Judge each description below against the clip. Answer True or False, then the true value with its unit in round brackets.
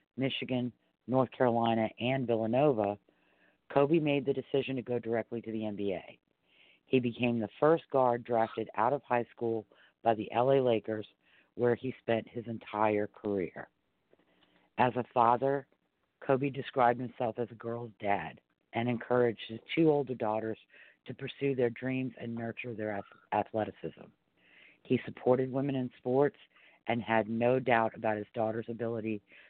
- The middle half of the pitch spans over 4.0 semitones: False (2.7 semitones)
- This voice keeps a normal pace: True (145 wpm)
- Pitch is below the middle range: True (120 Hz)